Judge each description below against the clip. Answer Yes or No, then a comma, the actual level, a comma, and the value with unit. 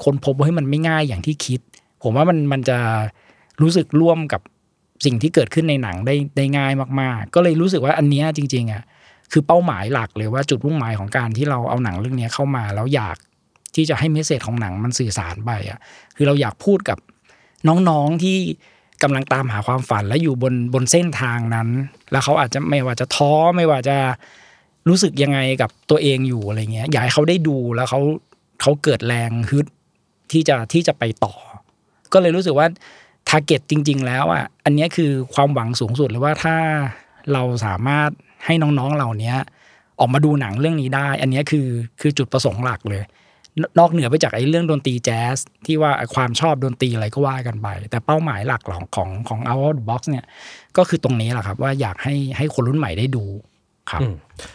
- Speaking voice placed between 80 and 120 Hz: No, low, 135 Hz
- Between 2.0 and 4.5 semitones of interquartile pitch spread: Yes, average, 4.0 semitones